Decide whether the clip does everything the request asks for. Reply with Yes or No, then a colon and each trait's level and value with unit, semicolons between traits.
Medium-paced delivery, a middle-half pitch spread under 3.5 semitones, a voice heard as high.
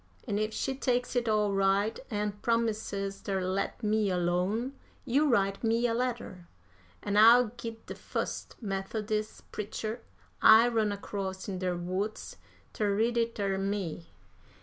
Yes: average, 150 wpm; average, 2.8 semitones; high, 210 Hz